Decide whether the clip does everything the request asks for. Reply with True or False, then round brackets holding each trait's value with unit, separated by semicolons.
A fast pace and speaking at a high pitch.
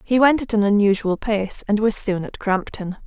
True (215 wpm; 210 Hz)